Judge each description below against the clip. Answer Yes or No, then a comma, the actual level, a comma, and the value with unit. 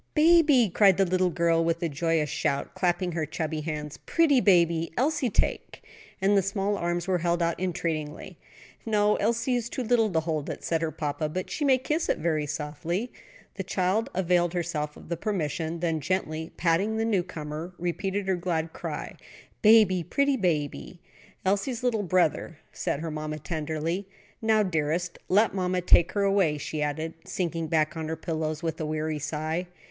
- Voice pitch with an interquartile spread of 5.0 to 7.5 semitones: No, average, 3.9 semitones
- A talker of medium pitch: Yes, medium, 175 Hz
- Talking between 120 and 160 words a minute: No, average, 175 wpm